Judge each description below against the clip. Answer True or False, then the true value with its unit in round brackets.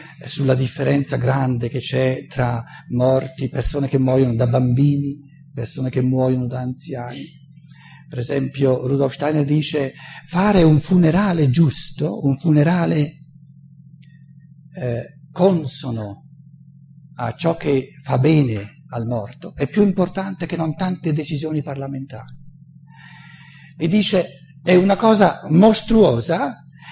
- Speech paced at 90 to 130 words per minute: True (115 wpm)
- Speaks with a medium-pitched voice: True (145 Hz)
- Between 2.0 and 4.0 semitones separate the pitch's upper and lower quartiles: True (2.9 semitones)